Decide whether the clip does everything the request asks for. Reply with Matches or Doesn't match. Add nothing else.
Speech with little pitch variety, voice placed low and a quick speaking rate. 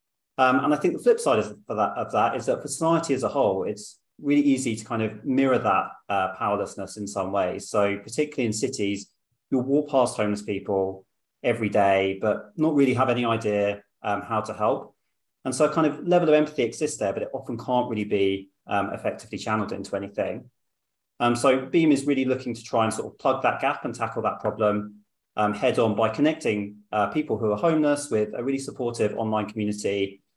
Doesn't match